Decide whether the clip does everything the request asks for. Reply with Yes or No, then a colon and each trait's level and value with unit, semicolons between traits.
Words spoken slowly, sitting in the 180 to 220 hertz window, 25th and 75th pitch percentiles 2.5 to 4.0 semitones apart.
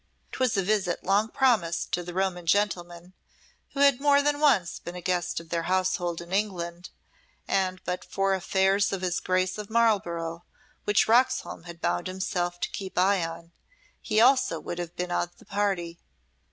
No: average, 175 wpm; medium, 185 Hz; average, 3.0 semitones